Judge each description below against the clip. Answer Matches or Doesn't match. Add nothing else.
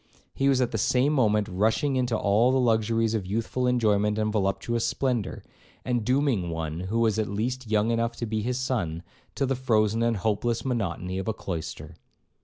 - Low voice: Matches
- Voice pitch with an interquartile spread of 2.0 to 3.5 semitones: Matches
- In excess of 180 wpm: Matches